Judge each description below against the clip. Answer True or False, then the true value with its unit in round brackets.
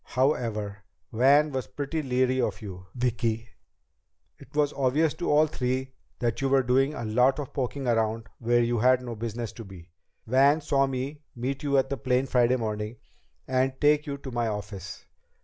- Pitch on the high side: False (125 Hz)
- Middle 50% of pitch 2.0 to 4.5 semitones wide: True (3.0 semitones)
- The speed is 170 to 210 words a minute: True (180 wpm)